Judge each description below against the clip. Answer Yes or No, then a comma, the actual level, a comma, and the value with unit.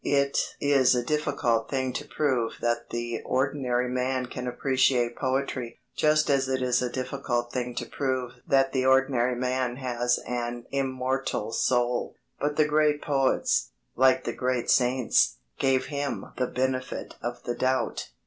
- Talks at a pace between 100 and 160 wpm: Yes, average, 150 wpm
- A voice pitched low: Yes, low, 130 Hz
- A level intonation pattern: Yes, narrow, 1.8 semitones